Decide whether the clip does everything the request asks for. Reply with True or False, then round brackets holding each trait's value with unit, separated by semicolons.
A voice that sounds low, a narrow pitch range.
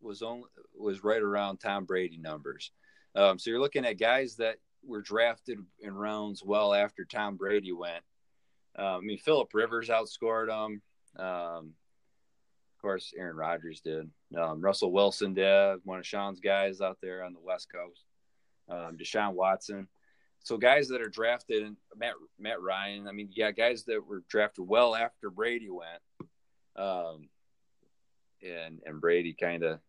False (100 Hz; 3.4 semitones)